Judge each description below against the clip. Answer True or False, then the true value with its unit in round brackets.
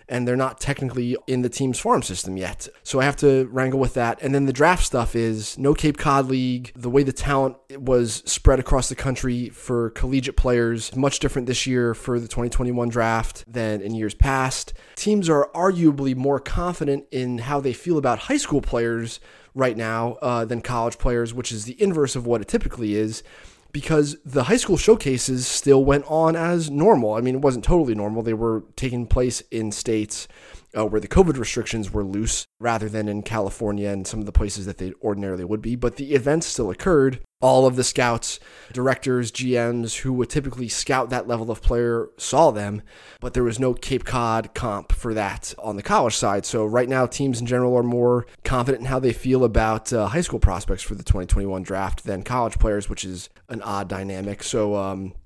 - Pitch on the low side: True (120 Hz)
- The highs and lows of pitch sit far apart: False (3.3 semitones)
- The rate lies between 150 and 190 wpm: False (205 wpm)